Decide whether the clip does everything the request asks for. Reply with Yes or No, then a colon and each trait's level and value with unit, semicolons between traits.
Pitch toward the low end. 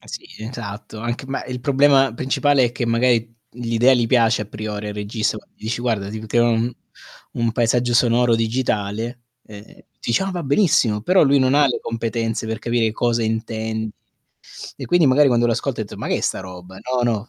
Yes: low, 115 Hz